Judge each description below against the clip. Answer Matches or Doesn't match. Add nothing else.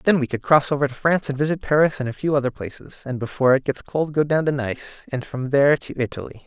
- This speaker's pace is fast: Matches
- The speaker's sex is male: Matches